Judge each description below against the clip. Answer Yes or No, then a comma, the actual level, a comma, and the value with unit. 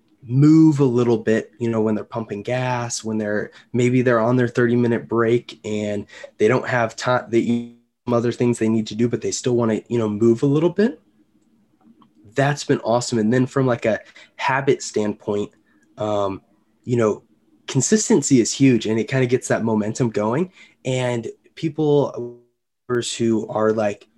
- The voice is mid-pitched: No, low, 120 Hz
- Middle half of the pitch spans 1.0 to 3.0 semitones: Yes, average, 2.7 semitones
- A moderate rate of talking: Yes, average, 180 wpm